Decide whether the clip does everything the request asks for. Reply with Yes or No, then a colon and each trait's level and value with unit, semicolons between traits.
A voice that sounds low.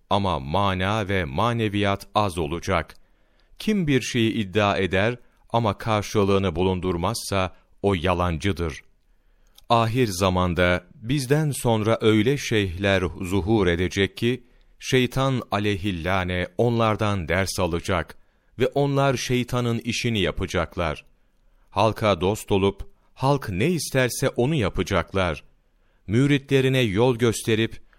Yes: low, 100 Hz